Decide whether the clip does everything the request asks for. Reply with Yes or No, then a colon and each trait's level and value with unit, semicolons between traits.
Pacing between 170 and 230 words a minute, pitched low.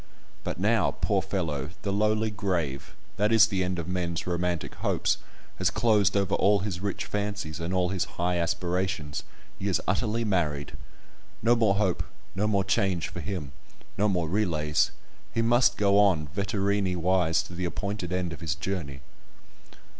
No: average, 160 wpm; very low, 95 Hz